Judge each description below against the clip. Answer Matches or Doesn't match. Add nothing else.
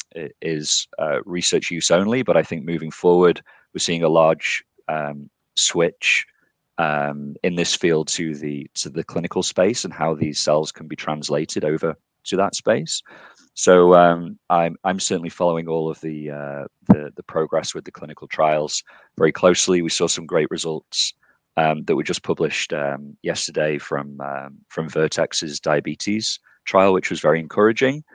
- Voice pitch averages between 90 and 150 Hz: Doesn't match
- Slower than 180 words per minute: Matches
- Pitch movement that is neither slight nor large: Doesn't match